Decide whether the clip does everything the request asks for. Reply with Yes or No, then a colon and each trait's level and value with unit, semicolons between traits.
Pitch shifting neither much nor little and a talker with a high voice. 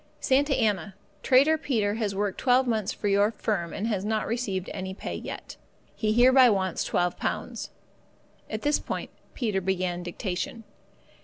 Yes: average, 4.2 semitones; high, 210 Hz